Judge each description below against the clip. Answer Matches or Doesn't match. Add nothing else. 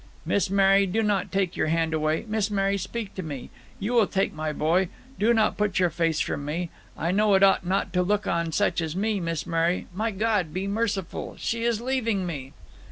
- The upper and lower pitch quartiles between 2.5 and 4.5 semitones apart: Matches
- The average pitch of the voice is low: Doesn't match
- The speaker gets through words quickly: Matches